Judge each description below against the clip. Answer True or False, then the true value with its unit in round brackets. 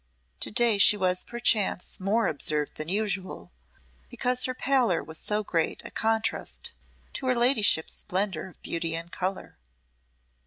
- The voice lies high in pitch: True (200 Hz)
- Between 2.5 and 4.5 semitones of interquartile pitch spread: False (5.1 semitones)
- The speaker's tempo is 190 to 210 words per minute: False (145 wpm)